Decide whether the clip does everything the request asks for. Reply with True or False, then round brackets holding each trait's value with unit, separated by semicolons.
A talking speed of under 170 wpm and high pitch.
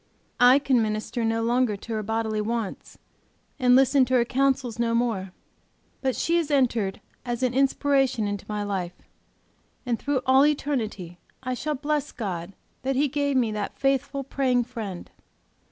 True (160 wpm; 245 Hz)